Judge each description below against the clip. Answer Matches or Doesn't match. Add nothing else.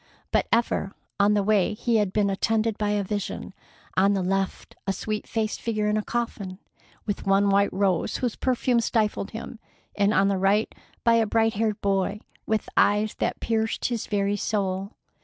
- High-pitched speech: Matches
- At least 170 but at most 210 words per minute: Matches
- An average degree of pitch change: Doesn't match